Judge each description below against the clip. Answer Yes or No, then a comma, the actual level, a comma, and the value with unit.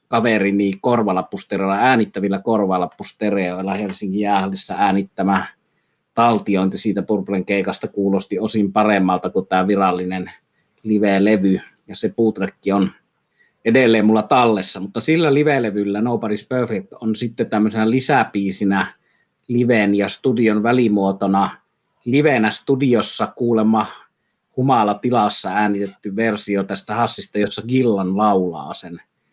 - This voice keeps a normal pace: Yes, average, 110 wpm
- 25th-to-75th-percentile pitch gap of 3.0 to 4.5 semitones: No, narrow, 2.5 semitones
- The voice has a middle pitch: No, low, 105 Hz